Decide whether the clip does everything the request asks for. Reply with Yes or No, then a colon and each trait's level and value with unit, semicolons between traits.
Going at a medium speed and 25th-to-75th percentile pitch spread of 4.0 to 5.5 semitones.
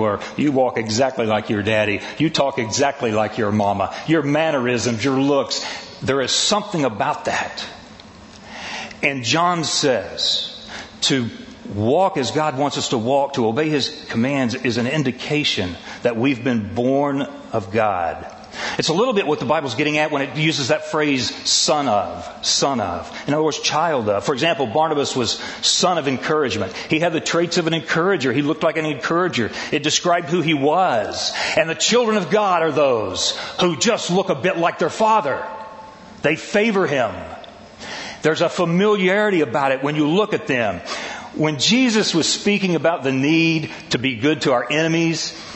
Yes: average, 175 wpm; average, 4.5 semitones